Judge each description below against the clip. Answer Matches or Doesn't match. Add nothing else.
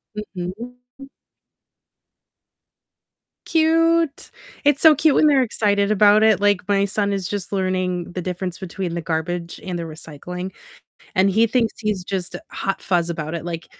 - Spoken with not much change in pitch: Doesn't match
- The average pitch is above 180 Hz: Matches